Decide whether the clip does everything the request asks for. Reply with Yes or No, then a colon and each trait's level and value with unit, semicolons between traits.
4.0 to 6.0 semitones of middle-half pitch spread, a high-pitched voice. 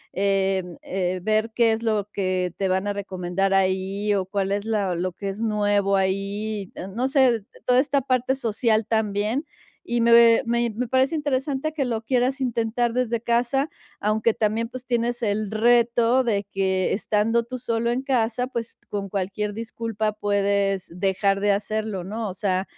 No: average, 3.2 semitones; high, 215 Hz